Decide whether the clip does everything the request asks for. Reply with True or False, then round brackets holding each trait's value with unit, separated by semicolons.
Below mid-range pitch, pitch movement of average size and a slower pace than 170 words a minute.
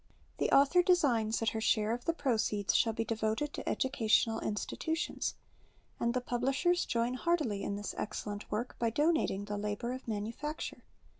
False (235 Hz; 4.7 semitones; 160 wpm)